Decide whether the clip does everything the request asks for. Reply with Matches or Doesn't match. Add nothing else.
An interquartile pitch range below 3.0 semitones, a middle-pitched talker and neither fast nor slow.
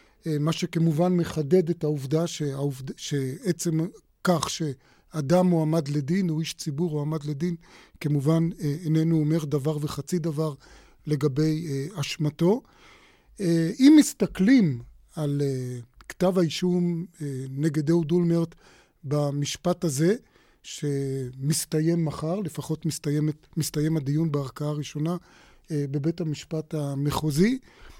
Doesn't match